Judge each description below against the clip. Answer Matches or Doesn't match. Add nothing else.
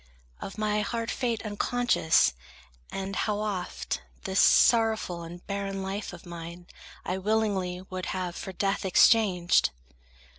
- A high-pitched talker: Matches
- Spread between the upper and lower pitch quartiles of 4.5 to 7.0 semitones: Doesn't match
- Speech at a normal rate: Doesn't match